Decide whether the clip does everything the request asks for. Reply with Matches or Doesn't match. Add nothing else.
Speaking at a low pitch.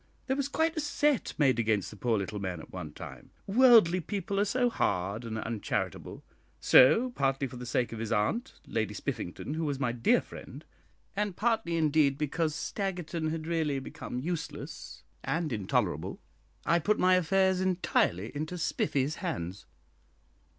Doesn't match